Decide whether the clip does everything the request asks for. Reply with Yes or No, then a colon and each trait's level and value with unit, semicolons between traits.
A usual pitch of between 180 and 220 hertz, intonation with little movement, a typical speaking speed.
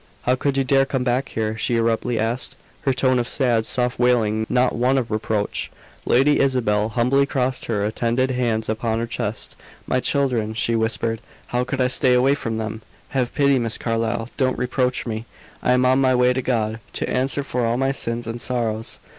No: low, 125 Hz; narrow, 2.3 semitones; average, 195 wpm